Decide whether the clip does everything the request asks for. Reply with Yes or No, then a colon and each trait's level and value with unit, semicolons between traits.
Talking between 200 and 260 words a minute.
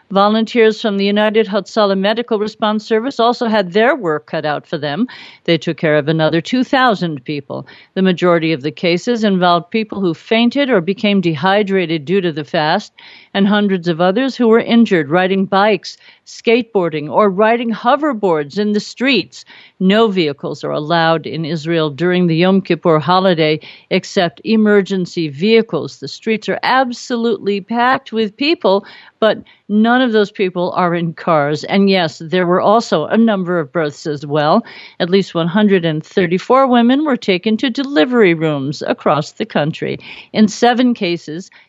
No: average, 160 wpm